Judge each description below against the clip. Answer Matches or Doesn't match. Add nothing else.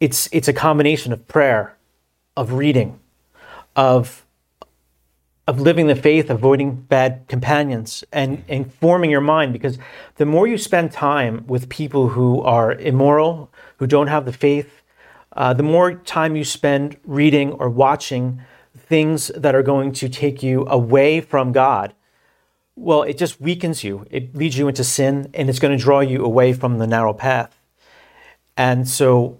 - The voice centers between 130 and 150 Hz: Matches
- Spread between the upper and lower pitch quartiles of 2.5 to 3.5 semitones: Matches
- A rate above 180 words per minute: Doesn't match